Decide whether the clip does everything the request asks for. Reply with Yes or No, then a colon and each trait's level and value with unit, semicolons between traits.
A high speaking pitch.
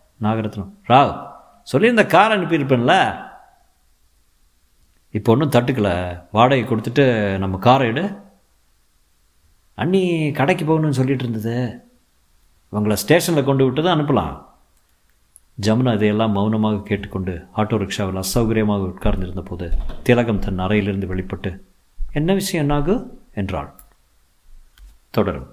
No: low, 105 Hz